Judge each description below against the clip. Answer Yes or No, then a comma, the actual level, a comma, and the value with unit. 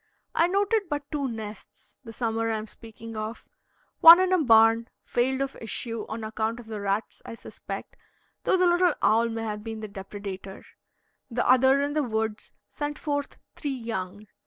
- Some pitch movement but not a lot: Yes, average, 4.7 semitones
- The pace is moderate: Yes, average, 180 wpm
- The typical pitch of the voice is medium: No, high, 230 Hz